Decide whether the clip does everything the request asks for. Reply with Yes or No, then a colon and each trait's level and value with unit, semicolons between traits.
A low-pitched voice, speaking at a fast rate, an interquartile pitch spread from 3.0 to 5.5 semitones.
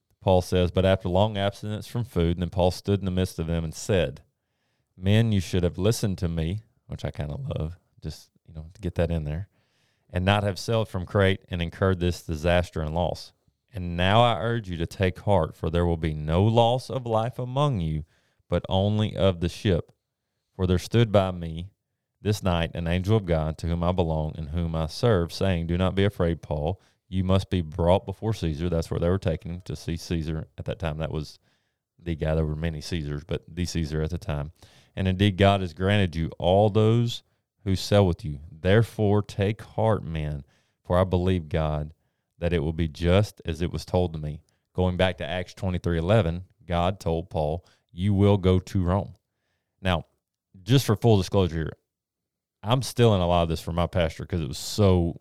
Yes: very low, 90 Hz; fast, 215 wpm; average, 3.5 semitones